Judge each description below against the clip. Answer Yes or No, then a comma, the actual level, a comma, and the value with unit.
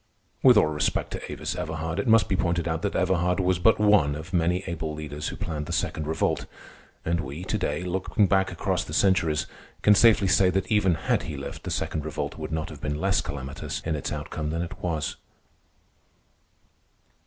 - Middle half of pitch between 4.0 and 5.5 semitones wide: No, average, 3.5 semitones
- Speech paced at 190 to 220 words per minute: Yes, average, 200 wpm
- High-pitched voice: No, very low, 85 Hz